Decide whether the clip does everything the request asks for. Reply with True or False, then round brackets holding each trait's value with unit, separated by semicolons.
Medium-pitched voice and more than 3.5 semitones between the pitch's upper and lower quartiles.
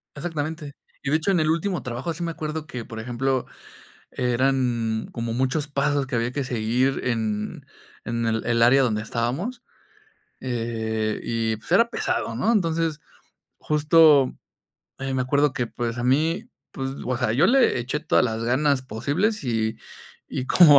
False (130 Hz; 4.7 semitones)